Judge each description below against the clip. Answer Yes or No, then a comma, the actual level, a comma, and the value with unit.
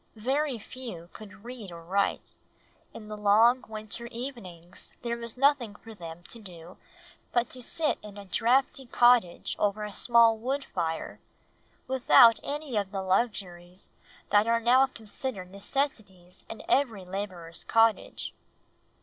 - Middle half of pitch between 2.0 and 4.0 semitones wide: No, average, 4.4 semitones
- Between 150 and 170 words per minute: No, average, 140 wpm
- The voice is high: Yes, high, 220 Hz